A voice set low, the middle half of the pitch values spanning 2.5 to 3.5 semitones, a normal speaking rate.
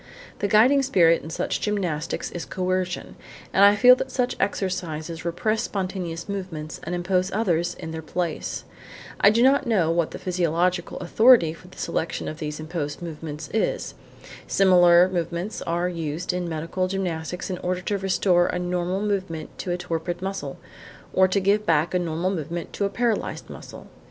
No: medium, 180 Hz; average, 2.8 semitones; average, 170 wpm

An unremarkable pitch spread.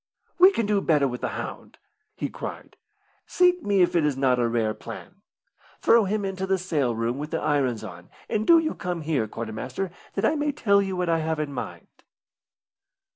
No: wide, 7.7 semitones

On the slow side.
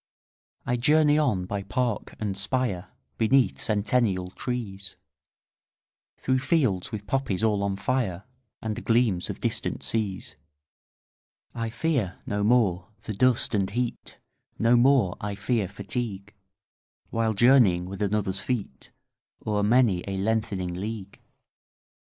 Yes: slow, 125 wpm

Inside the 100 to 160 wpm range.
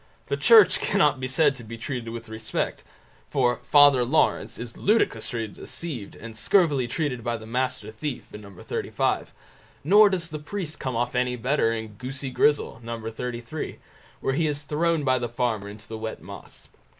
No: average, 175 wpm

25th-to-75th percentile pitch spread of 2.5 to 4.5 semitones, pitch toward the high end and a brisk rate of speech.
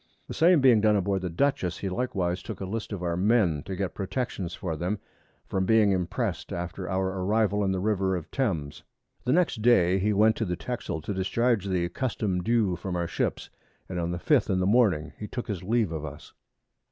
No: average, 3.7 semitones; very low, 95 Hz; fast, 215 wpm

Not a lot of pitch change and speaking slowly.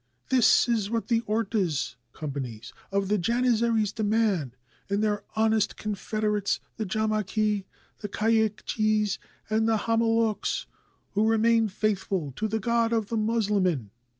Yes: narrow, 2.1 semitones; slow, 130 wpm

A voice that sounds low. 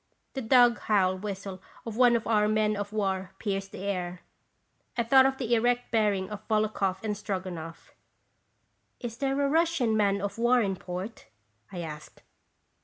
No: high, 210 Hz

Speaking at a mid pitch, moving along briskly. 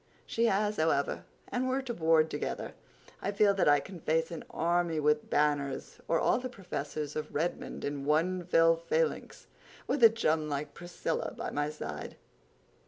No: medium, 165 Hz; average, 160 wpm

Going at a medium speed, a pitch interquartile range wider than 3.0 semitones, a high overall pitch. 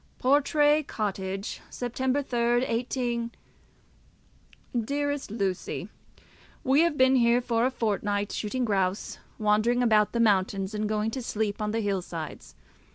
No: slow, 130 wpm; average, 3.7 semitones; high, 230 Hz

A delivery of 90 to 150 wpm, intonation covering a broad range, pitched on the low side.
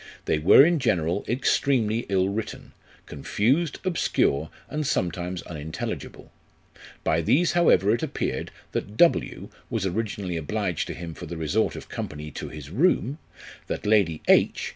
Yes: average, 140 wpm; wide, 7.3 semitones; low, 100 Hz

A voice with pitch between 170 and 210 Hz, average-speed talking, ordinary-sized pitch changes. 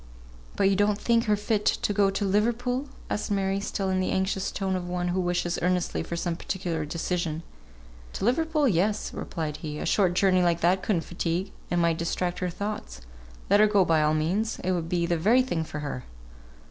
No: medium, 185 Hz; fast, 210 wpm; average, 3.3 semitones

